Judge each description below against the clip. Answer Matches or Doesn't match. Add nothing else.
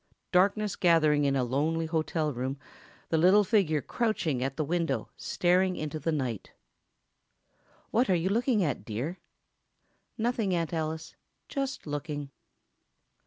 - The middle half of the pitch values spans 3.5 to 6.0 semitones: Matches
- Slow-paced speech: Matches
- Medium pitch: Matches